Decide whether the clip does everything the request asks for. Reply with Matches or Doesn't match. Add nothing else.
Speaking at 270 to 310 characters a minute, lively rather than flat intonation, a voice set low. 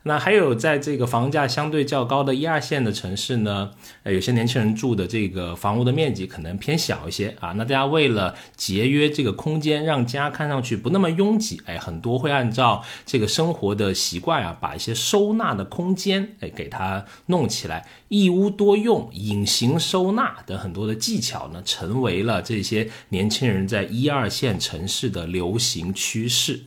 Matches